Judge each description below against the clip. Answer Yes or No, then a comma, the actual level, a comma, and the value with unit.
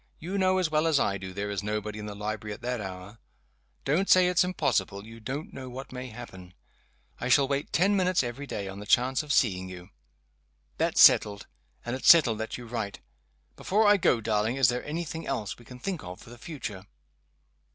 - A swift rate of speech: Yes, fast, 215 wpm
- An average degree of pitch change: No, wide, 6.5 semitones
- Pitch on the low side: Yes, low, 120 Hz